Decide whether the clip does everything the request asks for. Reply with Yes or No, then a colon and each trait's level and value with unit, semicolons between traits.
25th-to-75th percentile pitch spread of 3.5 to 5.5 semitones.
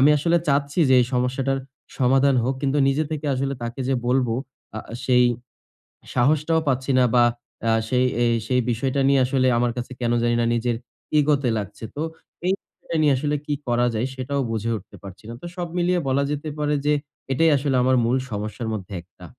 No: average, 2.9 semitones